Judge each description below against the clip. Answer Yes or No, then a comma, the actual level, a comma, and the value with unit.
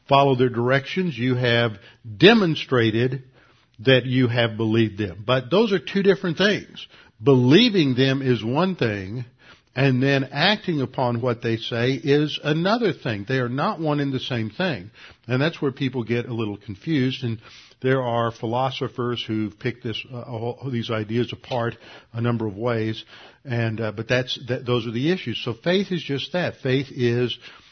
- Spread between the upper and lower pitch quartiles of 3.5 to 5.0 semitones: No, average, 3.0 semitones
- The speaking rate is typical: Yes, average, 175 wpm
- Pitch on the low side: Yes, low, 125 Hz